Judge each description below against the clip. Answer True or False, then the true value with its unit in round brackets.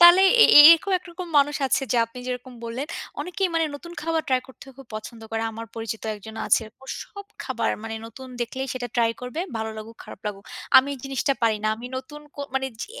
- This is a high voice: True (260 Hz)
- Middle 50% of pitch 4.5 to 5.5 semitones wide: True (4.8 semitones)